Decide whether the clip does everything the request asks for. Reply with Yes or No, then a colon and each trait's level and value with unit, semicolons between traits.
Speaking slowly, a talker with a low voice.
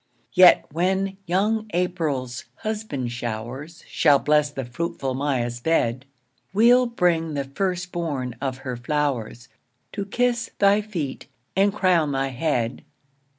No: slow, 125 wpm; medium, 150 Hz